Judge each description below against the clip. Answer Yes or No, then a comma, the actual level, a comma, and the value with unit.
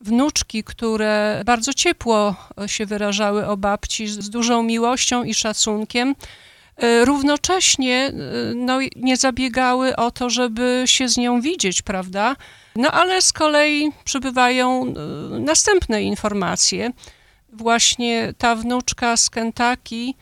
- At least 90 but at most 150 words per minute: Yes, slow, 110 wpm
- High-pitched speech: Yes, high, 240 Hz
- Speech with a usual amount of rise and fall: Yes, average, 3.1 semitones